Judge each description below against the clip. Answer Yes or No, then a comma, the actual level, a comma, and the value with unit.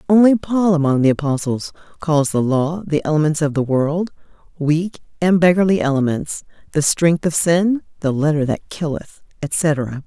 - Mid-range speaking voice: Yes, medium, 160 Hz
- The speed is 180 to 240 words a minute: No, average, 155 wpm